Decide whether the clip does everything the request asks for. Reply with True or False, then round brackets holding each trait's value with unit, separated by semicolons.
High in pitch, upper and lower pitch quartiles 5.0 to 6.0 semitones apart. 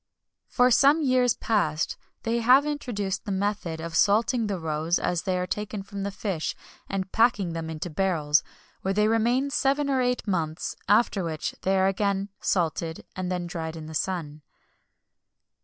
True (195 Hz; 5.3 semitones)